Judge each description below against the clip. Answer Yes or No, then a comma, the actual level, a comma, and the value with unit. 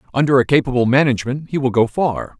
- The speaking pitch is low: Yes, low, 130 Hz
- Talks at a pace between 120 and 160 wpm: No, average, 200 wpm